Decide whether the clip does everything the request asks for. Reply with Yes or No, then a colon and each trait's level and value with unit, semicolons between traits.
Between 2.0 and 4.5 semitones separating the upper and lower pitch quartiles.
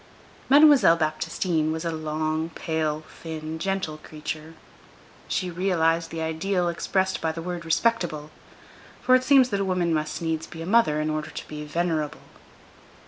Yes: average, 2.8 semitones